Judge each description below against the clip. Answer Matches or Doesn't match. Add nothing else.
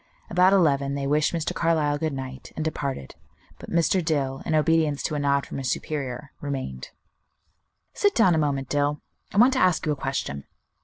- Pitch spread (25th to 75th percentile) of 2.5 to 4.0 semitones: Matches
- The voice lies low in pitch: Doesn't match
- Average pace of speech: Matches